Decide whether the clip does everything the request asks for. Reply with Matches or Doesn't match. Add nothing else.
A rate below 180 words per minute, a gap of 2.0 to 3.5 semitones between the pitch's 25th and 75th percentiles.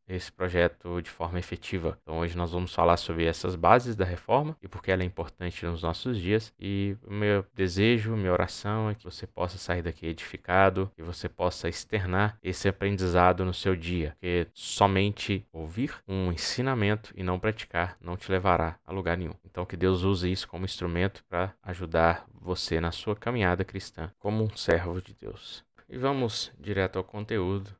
Doesn't match